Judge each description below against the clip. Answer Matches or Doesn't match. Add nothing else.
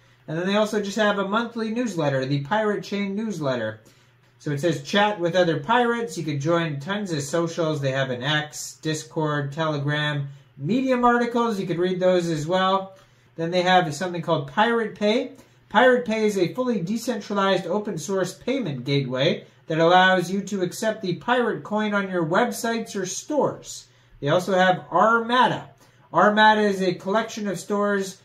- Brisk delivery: Doesn't match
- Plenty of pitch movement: Matches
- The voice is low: Doesn't match